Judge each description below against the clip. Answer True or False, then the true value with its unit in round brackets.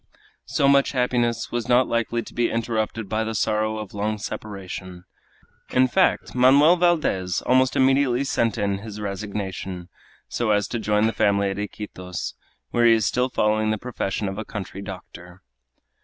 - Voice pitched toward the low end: True (110 Hz)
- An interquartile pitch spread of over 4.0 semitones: False (3.5 semitones)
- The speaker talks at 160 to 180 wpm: True (165 wpm)